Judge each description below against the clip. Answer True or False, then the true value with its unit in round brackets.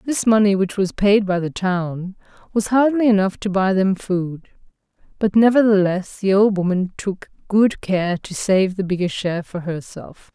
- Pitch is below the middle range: False (195 Hz)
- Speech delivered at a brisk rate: False (175 wpm)